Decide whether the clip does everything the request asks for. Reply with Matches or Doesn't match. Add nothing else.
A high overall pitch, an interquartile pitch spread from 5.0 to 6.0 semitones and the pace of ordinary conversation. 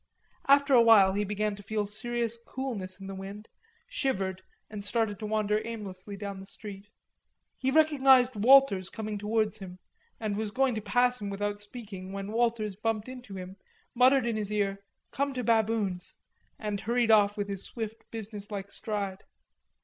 Doesn't match